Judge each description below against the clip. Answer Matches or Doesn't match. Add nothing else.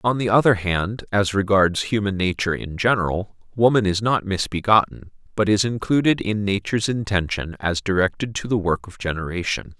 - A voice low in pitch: Matches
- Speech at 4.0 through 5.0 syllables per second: Doesn't match